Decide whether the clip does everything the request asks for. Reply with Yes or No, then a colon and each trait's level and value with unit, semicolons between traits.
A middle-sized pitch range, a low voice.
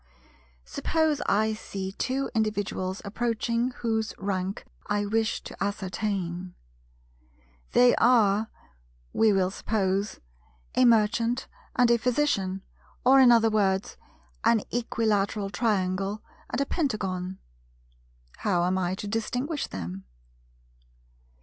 No: average, 3.5 semitones; high, 210 Hz